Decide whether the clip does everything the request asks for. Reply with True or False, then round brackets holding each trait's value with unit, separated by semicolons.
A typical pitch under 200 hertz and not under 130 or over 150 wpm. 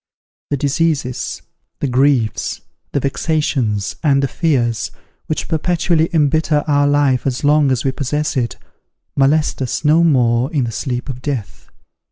True (140 Hz; 145 wpm)